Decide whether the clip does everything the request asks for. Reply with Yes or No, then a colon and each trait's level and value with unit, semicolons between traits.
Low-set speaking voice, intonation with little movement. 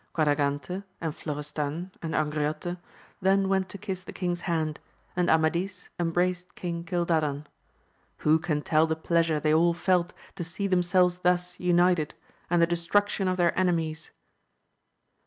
No: medium, 170 Hz; narrow, 2.3 semitones